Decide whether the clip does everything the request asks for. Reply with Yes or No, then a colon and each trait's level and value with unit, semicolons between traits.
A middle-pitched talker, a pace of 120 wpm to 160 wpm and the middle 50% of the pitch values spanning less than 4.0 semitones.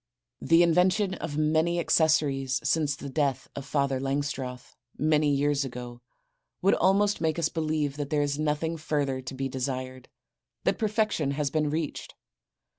Yes: medium, 150 Hz; average, 150 wpm; average, 2.8 semitones